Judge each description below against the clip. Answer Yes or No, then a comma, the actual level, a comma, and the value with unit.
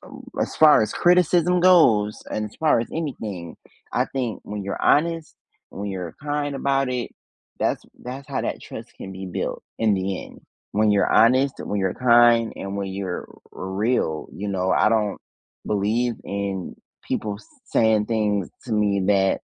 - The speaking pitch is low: Yes, low, 110 Hz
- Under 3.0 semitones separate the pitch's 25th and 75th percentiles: No, average, 4.8 semitones